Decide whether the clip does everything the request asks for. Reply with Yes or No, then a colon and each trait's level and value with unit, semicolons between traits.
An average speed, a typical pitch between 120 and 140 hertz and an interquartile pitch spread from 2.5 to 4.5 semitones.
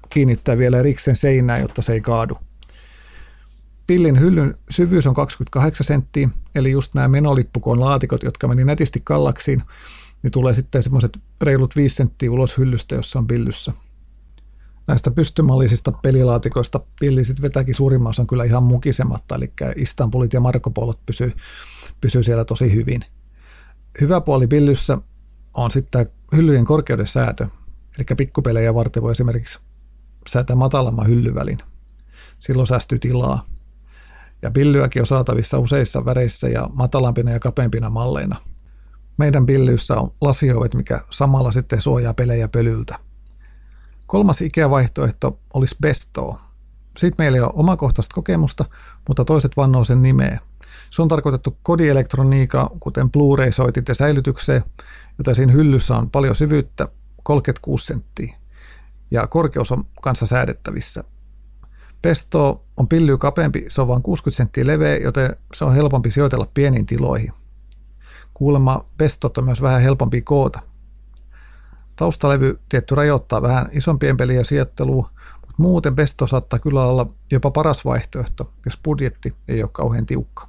Yes: average, 135 wpm; low, 130 Hz; average, 3.1 semitones